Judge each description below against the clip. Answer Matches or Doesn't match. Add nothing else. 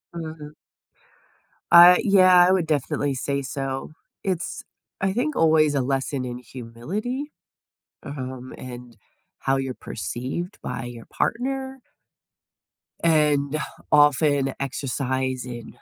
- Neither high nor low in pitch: Matches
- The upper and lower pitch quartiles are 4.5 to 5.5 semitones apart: Matches